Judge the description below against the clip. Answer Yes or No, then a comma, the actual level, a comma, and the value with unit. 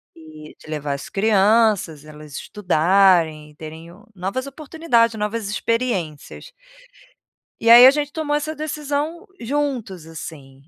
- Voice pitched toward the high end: Yes, high, 205 Hz